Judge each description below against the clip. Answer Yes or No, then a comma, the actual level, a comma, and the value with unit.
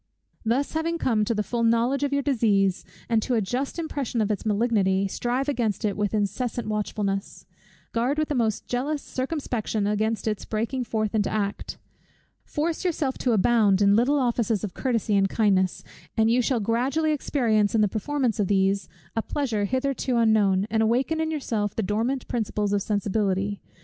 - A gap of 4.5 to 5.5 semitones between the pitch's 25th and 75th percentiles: No, average, 3.9 semitones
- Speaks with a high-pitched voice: Yes, high, 225 Hz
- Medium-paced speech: Yes, average, 175 wpm